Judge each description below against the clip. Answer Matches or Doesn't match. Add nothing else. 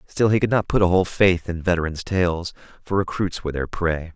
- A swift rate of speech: Matches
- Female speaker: Doesn't match